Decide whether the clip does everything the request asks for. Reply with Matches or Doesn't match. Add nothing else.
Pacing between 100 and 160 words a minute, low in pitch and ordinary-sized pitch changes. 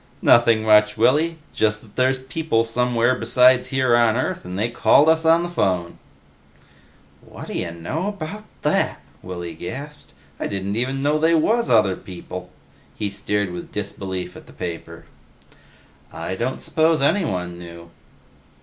Doesn't match